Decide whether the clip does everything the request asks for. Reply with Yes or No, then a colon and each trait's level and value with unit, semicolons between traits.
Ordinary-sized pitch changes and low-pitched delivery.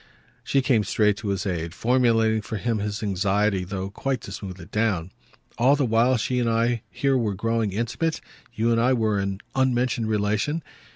Yes: average, 3.2 semitones; low, 110 Hz